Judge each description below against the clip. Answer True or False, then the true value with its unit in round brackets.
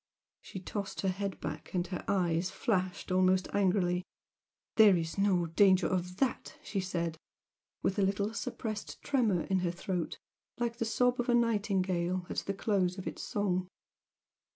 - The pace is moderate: True (155 wpm)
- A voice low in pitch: False (190 Hz)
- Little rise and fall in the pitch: True (2.3 semitones)